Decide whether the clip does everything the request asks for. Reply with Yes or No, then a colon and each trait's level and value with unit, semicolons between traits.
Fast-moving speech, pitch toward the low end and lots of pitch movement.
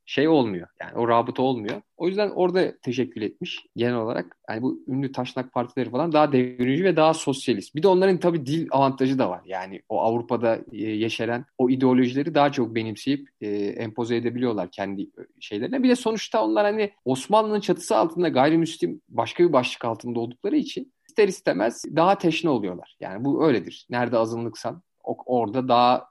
Yes: fast, 165 wpm; low, 130 Hz; wide, 5.8 semitones